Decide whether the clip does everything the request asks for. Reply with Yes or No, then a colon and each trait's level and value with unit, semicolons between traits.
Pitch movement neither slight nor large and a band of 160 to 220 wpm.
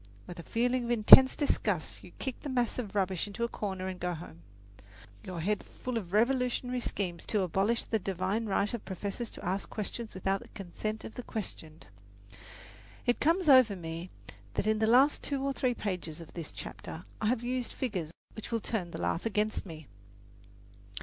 Yes: average, 4.7 semitones; average, 190 wpm